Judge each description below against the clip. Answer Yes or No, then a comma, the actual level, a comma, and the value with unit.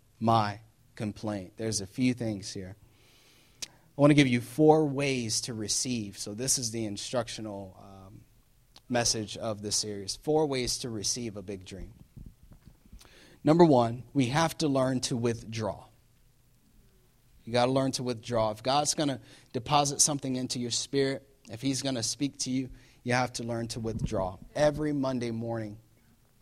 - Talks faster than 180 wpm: No, average, 165 wpm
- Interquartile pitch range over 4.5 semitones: No, average, 3.2 semitones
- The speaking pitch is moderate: No, low, 120 Hz